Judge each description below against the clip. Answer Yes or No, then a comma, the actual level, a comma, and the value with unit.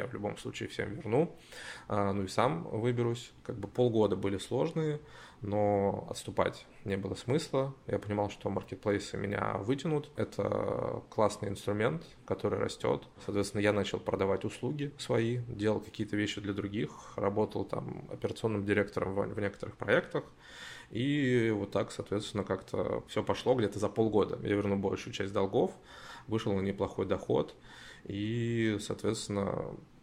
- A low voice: Yes, low, 105 Hz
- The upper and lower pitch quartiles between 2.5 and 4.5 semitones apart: Yes, average, 2.8 semitones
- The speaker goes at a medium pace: Yes, average, 140 wpm